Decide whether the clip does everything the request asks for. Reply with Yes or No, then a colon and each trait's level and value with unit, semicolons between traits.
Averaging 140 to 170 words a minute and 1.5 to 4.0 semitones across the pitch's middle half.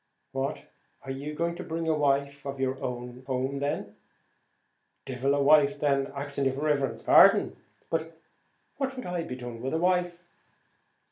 Yes: average, 150 wpm; average, 3.2 semitones